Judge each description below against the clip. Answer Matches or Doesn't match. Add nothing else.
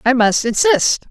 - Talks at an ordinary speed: Matches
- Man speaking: Doesn't match